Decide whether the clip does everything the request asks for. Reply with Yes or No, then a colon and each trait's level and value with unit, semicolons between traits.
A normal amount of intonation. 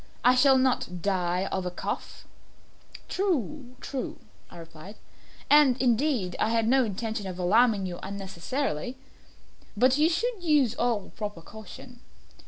No: wide, 5.8 semitones